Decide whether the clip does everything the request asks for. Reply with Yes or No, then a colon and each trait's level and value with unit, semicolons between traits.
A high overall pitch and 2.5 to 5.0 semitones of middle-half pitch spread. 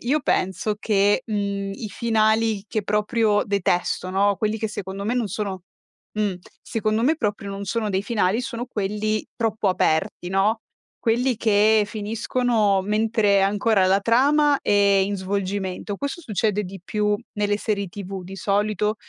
No: high, 210 Hz; narrow, 2.0 semitones